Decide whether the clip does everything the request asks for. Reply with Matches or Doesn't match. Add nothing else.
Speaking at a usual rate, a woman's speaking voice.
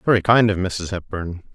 Doesn't match